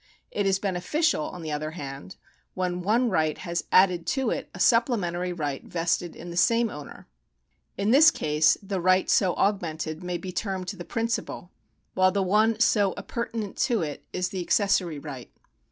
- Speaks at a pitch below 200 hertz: Yes, medium, 185 Hz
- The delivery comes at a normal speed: Yes, average, 175 wpm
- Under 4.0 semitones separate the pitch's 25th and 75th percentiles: Yes, average, 3.5 semitones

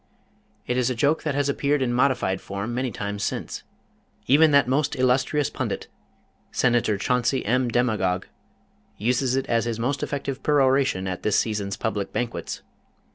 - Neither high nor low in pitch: No, low, 125 Hz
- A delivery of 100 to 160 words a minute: Yes, average, 150 wpm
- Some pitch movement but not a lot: Yes, average, 4.0 semitones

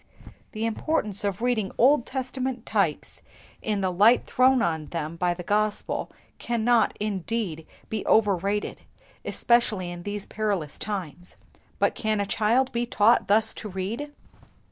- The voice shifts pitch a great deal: No, average, 3.9 semitones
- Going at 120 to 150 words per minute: Yes, average, 145 wpm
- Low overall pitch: No, high, 210 Hz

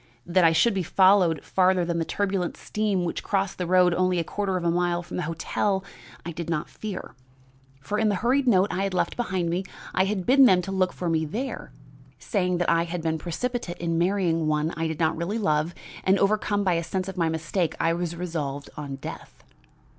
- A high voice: No, medium, 180 Hz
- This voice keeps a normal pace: No, fast, 220 wpm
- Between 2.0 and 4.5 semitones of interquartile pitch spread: Yes, average, 2.7 semitones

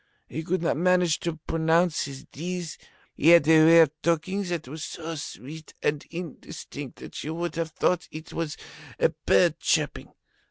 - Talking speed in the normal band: Yes, average, 170 wpm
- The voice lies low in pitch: No, medium, 165 Hz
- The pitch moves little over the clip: Yes, narrow, 1.7 semitones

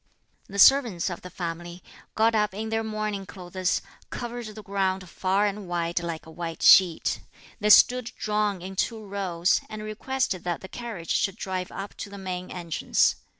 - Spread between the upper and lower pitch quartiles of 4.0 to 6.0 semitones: No, average, 3.2 semitones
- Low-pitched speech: No, high, 195 Hz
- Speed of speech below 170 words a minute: No, average, 175 wpm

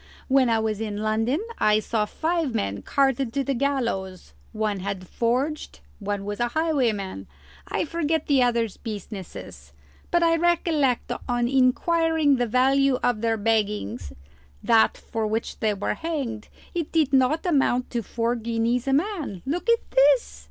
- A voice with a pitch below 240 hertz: No, high, 245 Hz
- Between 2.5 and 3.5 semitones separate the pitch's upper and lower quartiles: No, average, 4.8 semitones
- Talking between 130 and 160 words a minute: Yes, average, 155 wpm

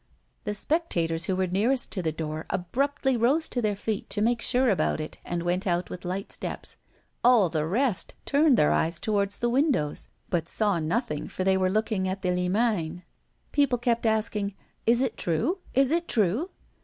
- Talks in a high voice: Yes, high, 205 Hz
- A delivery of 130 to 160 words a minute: No, average, 185 wpm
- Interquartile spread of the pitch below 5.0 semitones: No, average, 5.3 semitones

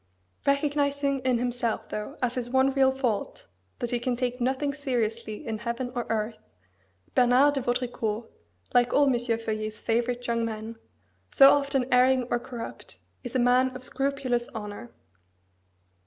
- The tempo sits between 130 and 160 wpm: Yes, average, 150 wpm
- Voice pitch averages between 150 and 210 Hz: No, high, 245 Hz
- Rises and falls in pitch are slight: Yes, narrow, 2.3 semitones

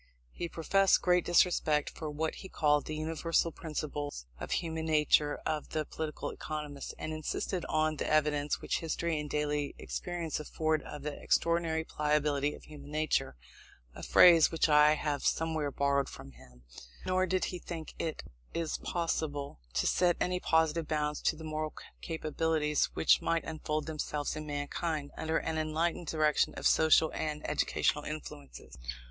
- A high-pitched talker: No, medium, 155 Hz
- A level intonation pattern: Yes, narrow, 1.5 semitones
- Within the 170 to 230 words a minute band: No, average, 155 wpm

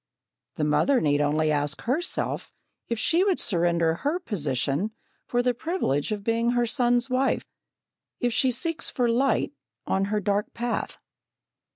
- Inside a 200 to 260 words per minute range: No, average, 150 wpm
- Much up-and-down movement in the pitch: Yes, wide, 7.2 semitones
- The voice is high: Yes, high, 230 Hz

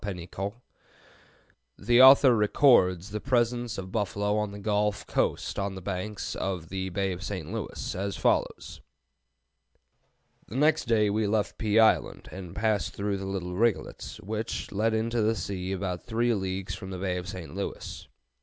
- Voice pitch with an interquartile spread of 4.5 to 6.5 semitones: No, average, 2.7 semitones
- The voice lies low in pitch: Yes, low, 100 Hz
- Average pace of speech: Yes, average, 165 wpm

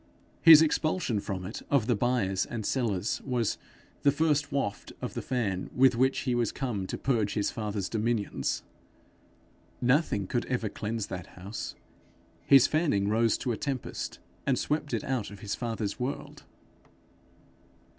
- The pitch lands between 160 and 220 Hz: No, low, 120 Hz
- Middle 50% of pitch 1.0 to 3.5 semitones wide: No, average, 4.5 semitones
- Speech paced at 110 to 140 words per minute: No, average, 155 wpm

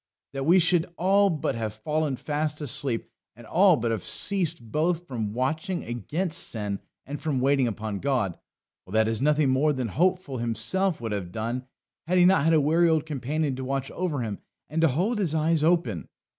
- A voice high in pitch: No, medium, 145 Hz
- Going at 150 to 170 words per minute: No, average, 195 wpm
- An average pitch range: No, wide, 5.9 semitones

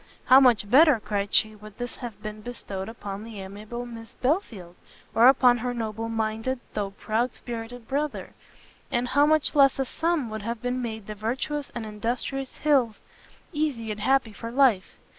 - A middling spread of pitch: Yes, average, 3.3 semitones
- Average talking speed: Yes, average, 170 wpm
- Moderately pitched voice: No, high, 235 Hz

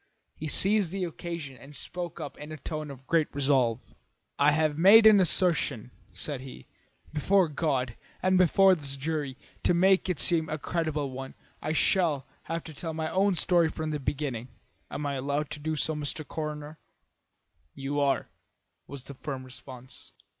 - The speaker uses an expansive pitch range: No, average, 3.4 semitones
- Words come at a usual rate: Yes, average, 170 wpm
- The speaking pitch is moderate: Yes, medium, 150 Hz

